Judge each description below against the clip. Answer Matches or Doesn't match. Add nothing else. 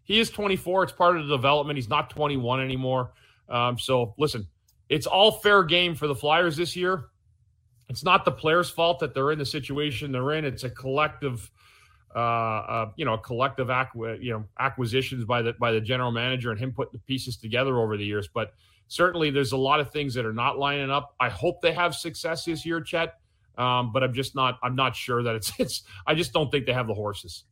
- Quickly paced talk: Matches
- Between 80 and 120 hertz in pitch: Doesn't match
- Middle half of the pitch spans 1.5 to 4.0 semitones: Doesn't match